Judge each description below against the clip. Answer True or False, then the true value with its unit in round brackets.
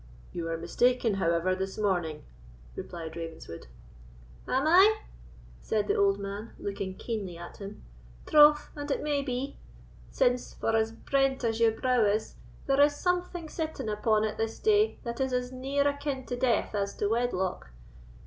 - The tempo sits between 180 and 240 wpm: False (160 wpm)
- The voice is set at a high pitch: True (230 Hz)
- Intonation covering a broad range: True (5.8 semitones)